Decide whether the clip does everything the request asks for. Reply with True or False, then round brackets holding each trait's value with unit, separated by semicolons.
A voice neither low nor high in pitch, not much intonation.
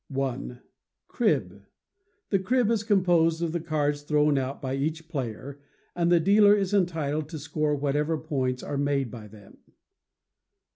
False (150 Hz; 3.7 semitones)